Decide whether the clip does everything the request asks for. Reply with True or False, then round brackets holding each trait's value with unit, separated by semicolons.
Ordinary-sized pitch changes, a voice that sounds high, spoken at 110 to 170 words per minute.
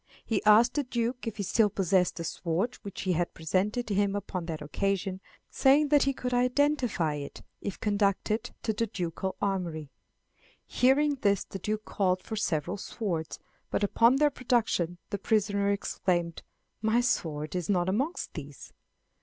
True (4.9 semitones; 200 Hz; 160 wpm)